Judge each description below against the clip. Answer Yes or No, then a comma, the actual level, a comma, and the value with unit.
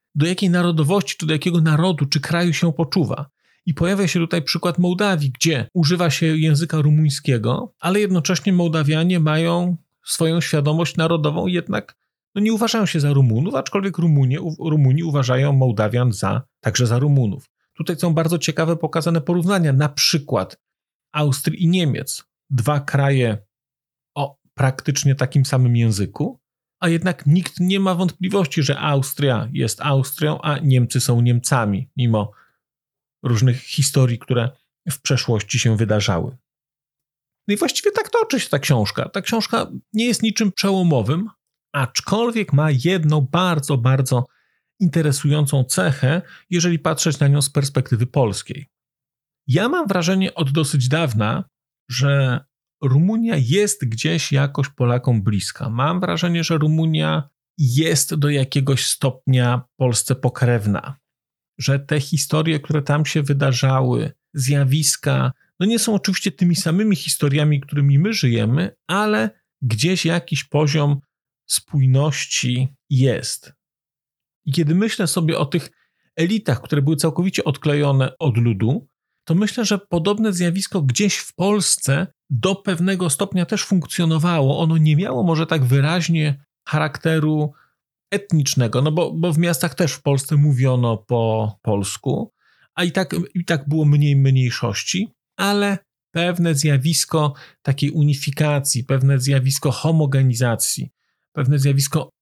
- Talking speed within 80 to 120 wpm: No, average, 130 wpm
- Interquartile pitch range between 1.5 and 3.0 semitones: No, average, 4.3 semitones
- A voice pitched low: No, medium, 150 Hz